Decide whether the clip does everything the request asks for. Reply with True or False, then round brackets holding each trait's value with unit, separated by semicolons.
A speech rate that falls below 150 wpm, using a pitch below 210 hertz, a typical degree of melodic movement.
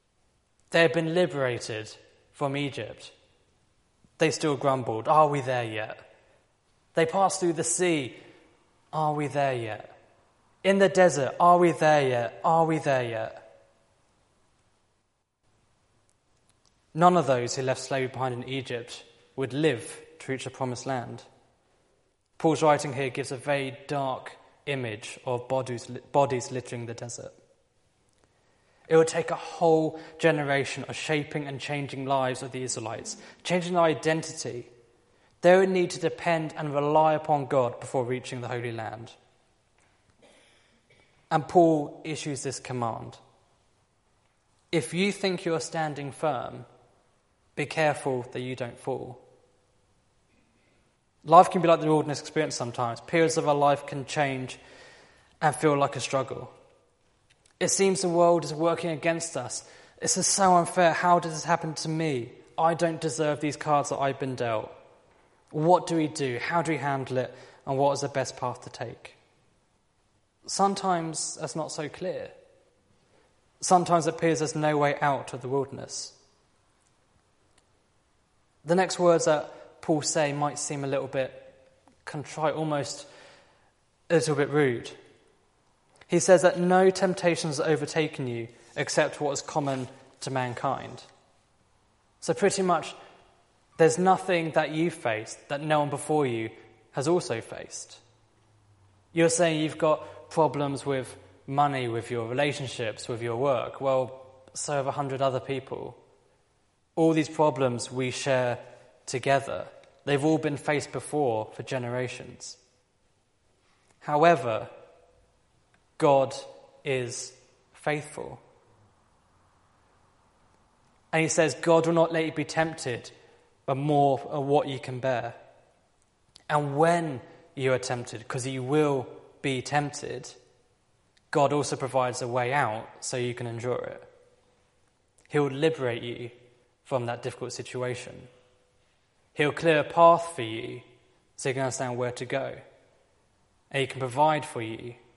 True (140 wpm; 135 Hz; 4.5 semitones)